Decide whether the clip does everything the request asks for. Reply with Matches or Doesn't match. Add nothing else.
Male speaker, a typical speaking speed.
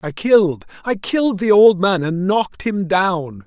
Matches